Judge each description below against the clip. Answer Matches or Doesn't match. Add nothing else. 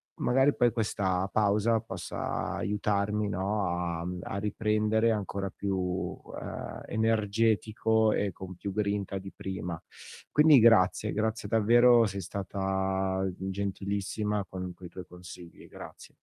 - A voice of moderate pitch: Doesn't match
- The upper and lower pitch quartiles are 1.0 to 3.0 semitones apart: Matches